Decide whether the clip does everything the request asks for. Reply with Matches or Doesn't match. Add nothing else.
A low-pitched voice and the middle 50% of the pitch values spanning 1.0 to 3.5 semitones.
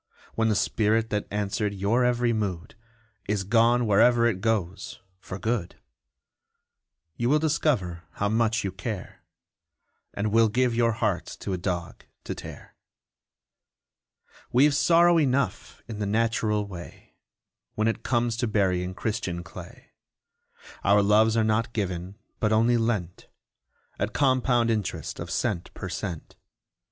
Matches